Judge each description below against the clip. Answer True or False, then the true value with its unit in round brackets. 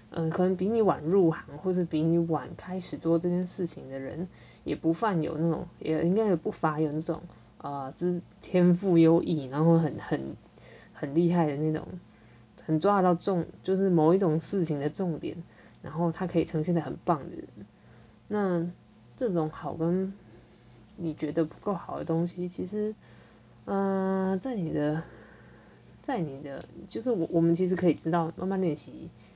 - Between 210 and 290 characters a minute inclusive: True (245 characters per minute)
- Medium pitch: True (170 Hz)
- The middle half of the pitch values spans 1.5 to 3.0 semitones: True (2.7 semitones)